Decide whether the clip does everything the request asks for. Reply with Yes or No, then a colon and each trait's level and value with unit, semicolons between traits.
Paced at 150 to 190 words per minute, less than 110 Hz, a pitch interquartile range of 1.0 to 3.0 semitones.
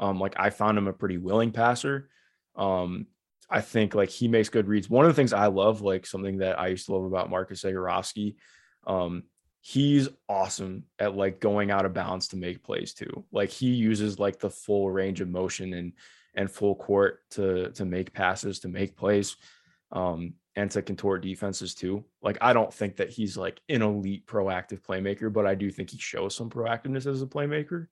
No: average, 200 wpm; low, 100 Hz; narrow, 2.4 semitones